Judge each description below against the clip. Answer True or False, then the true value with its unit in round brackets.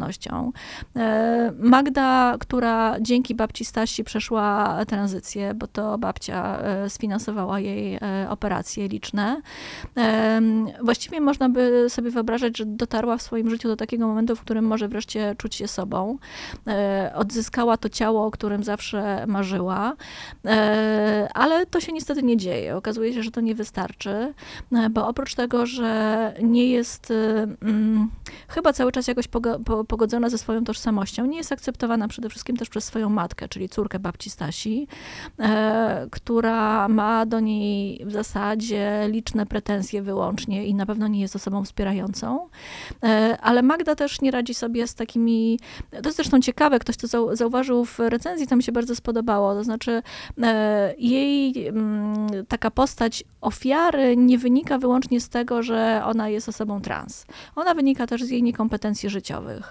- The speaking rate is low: False (150 wpm)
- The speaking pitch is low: False (225 Hz)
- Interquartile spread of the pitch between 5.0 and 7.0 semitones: False (2.4 semitones)